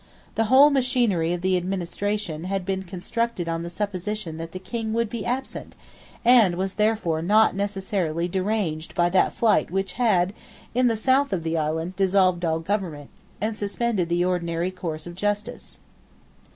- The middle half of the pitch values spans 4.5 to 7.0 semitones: No, average, 3.7 semitones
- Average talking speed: Yes, average, 165 wpm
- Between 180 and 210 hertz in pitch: Yes, high, 190 Hz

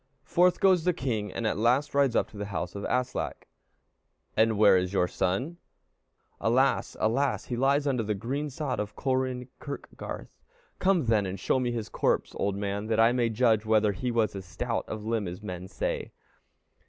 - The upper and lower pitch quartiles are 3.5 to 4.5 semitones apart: Yes, average, 4.2 semitones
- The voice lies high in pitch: No, low, 115 Hz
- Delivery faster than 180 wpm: Yes, average, 190 wpm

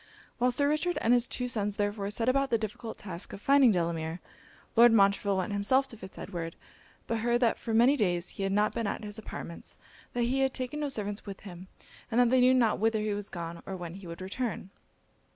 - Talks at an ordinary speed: No, fast, 225 wpm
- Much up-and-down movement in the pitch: No, average, 4.0 semitones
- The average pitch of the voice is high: Yes, high, 215 Hz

